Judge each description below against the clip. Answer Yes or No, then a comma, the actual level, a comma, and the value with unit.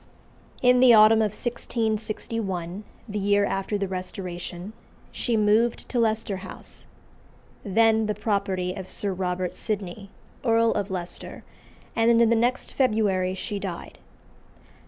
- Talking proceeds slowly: Yes, slow, 130 wpm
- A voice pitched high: Yes, high, 210 Hz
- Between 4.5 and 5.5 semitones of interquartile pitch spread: No, average, 3.1 semitones